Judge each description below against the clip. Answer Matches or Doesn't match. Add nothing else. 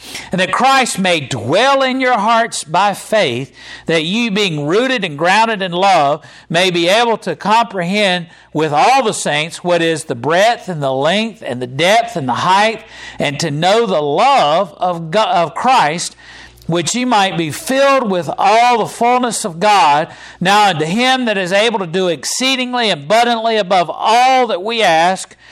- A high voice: Matches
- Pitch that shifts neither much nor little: Doesn't match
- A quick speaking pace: Doesn't match